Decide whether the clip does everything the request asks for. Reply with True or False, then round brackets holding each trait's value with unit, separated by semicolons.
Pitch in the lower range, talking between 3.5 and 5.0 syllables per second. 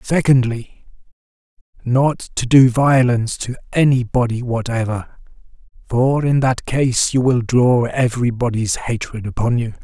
True (125 Hz; 4.3 syllables/s)